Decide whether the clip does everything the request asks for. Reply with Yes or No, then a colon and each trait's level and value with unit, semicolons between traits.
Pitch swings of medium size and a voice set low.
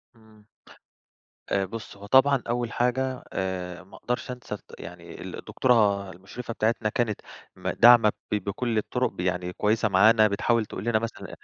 Yes: average, 3.2 semitones; low, 110 Hz